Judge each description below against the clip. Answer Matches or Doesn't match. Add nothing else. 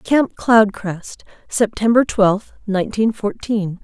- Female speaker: Matches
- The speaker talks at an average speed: Doesn't match